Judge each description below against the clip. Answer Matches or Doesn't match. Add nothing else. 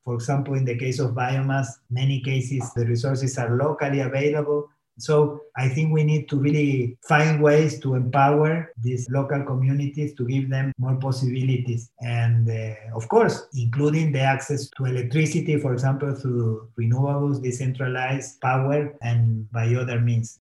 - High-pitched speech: Doesn't match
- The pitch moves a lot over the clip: Doesn't match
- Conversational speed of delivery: Matches